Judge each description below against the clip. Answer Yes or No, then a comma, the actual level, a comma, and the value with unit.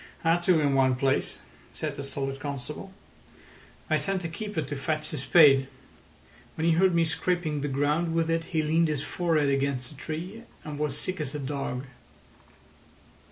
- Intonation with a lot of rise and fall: No, average, 3.2 semitones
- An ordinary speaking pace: Yes, average, 180 wpm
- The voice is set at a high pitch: No, medium, 150 Hz